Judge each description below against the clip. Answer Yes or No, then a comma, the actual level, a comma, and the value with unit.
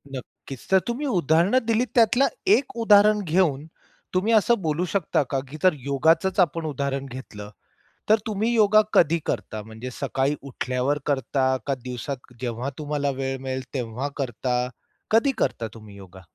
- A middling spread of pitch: No, wide, 7.4 semitones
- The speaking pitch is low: No, medium, 145 Hz